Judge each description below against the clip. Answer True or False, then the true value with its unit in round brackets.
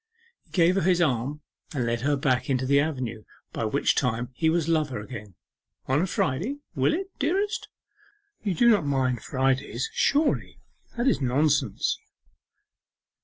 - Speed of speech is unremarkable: True (150 wpm)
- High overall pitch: False (140 Hz)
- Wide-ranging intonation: True (5.8 semitones)